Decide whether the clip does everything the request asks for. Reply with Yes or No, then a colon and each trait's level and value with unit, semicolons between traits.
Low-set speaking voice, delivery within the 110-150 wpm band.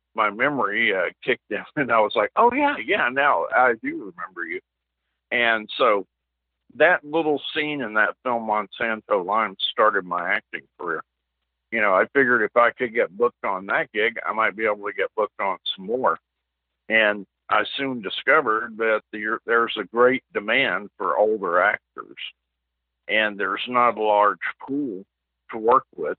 No: low, 110 Hz; average, 170 wpm